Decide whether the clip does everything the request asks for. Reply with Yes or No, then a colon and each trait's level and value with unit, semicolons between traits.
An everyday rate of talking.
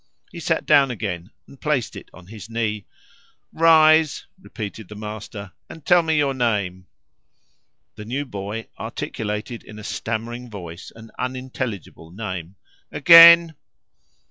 No: slow, 130 wpm